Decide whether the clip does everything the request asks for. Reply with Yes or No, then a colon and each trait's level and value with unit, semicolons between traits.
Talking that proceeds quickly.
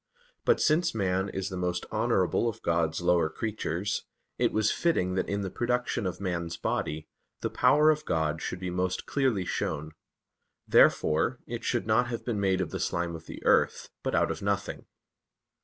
No: average, 180 wpm